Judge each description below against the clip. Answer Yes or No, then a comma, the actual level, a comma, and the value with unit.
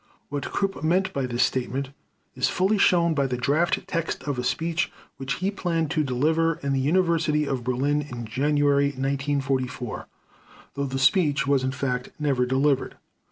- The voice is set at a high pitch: No, medium, 140 Hz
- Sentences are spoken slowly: No, average, 165 wpm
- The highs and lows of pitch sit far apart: No, average, 3.7 semitones